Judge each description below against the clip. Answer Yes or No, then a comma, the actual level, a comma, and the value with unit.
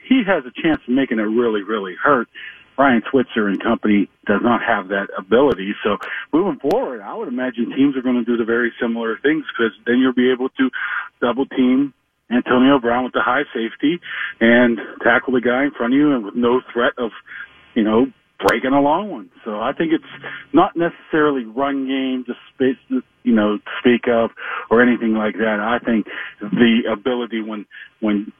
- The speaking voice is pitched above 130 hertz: No, low, 125 Hz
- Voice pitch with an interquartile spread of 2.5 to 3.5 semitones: Yes, average, 2.9 semitones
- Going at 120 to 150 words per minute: No, average, 190 wpm